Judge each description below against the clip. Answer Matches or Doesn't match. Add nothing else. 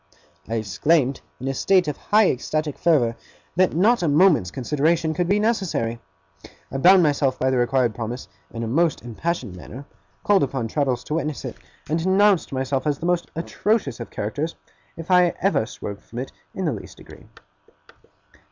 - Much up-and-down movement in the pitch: Matches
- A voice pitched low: Doesn't match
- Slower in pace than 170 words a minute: Doesn't match